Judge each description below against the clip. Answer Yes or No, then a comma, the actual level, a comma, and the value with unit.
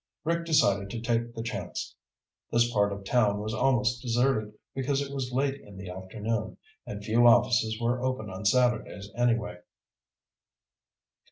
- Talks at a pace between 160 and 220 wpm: No, average, 150 wpm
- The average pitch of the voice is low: Yes, low, 115 Hz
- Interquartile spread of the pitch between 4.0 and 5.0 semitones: No, average, 3.3 semitones